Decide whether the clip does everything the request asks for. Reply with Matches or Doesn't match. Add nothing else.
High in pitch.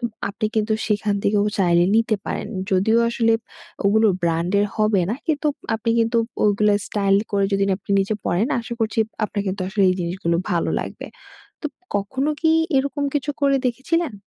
Matches